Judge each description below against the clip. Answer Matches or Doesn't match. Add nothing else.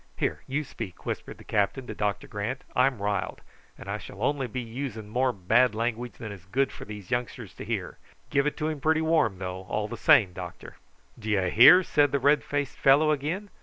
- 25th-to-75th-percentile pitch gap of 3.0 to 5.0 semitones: Doesn't match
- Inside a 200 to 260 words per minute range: Matches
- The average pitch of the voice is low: Matches